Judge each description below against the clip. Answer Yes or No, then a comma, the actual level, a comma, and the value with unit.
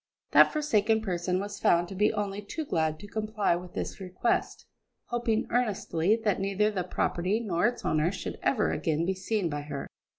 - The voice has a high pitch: Yes, high, 195 Hz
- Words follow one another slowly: No, average, 185 wpm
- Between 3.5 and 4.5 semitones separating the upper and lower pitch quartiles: Yes, average, 3.8 semitones